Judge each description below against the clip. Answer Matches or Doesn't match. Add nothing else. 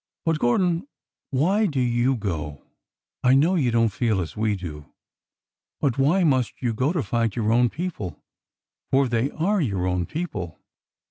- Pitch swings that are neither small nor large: Doesn't match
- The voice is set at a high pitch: Doesn't match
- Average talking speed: Matches